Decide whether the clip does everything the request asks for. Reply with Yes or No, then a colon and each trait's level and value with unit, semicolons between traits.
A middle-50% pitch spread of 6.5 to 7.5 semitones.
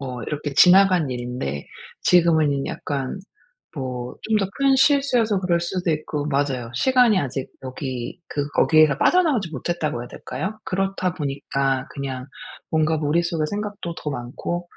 No: wide, 5.6 semitones